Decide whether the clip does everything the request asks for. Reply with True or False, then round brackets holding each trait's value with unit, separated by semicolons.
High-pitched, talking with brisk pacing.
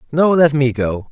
False (140 Hz; 215 wpm)